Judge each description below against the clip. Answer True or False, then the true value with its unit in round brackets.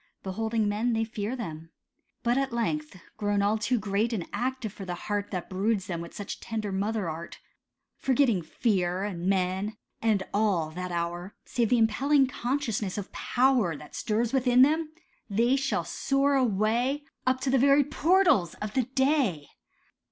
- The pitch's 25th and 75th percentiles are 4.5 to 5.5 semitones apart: True (5.1 semitones)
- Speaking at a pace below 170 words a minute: True (160 wpm)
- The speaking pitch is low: False (220 Hz)